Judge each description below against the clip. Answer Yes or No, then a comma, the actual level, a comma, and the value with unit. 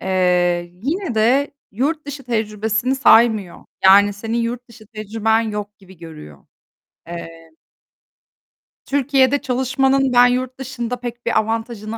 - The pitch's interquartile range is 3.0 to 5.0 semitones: Yes, average, 4.0 semitones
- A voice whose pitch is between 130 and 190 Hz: No, high, 230 Hz